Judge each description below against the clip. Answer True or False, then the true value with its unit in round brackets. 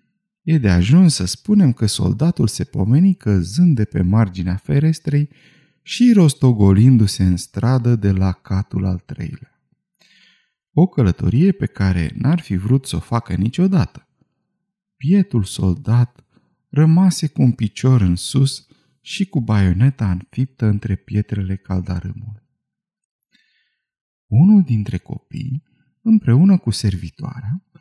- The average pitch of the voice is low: True (130 Hz)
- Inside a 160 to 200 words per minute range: False (120 wpm)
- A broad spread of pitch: True (8.7 semitones)